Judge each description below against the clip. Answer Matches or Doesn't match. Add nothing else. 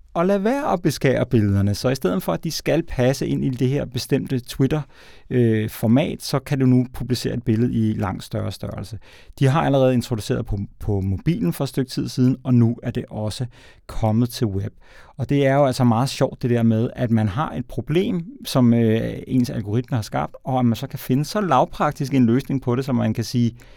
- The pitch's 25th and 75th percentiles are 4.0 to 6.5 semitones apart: Doesn't match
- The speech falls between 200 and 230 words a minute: Matches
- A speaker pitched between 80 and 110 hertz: Doesn't match